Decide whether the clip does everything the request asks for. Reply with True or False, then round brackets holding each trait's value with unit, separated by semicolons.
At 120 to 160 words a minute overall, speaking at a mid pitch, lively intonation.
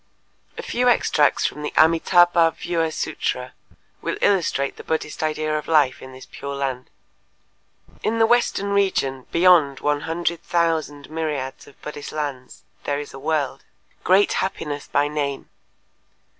False (145 wpm; 155 Hz; 3.3 semitones)